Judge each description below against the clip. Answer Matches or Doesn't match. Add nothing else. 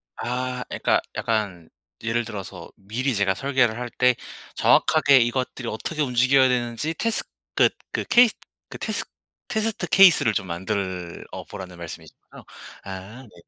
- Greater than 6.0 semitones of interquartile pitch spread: Doesn't match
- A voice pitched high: Doesn't match